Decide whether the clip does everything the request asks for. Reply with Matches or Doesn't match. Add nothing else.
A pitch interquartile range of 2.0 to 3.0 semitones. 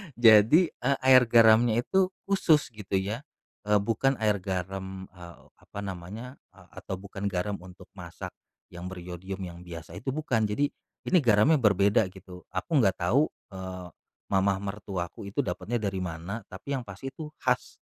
Doesn't match